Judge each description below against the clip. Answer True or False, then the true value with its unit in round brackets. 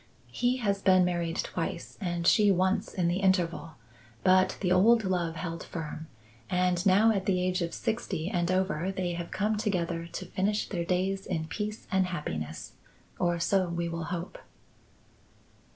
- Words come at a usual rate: True (165 wpm)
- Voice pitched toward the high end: False (180 Hz)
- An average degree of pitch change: False (2.2 semitones)